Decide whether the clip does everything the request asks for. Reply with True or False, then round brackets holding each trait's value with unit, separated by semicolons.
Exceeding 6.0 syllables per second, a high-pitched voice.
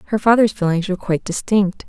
True (6.8 syllables/s; 200 Hz)